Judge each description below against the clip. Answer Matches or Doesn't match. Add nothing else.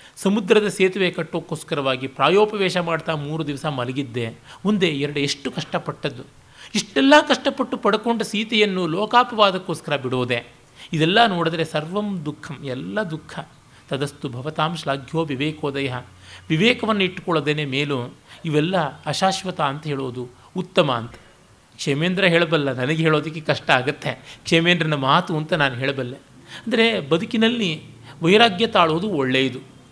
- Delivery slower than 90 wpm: Doesn't match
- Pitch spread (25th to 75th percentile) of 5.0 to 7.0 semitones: Matches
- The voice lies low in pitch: Doesn't match